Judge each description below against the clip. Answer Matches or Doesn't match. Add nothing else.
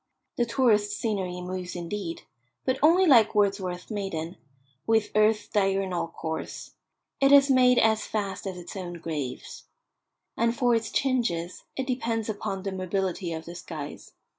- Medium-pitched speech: Doesn't match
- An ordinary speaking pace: Matches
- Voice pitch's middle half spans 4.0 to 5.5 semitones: Matches